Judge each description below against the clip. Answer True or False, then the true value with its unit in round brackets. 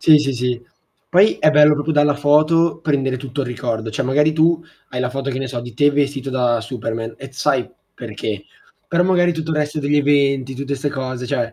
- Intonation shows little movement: False (3.1 semitones)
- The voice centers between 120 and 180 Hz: True (140 Hz)